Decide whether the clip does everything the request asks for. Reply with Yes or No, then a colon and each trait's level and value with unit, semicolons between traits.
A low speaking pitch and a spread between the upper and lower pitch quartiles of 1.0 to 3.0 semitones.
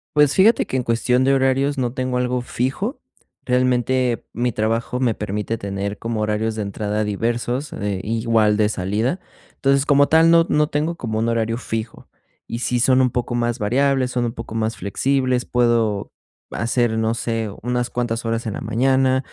Yes: low, 120 Hz; average, 2.7 semitones